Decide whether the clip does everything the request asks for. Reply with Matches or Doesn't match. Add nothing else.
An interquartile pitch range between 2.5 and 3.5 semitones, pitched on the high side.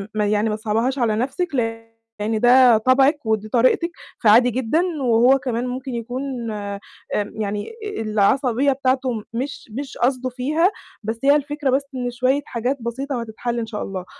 Matches